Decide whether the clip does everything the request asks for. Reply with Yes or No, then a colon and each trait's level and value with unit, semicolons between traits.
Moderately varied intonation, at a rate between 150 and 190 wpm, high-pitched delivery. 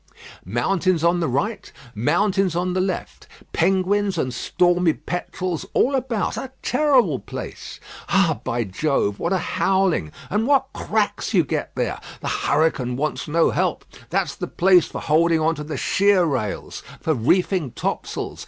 No: average, 4.2 semitones; average, 155 wpm; medium, 175 Hz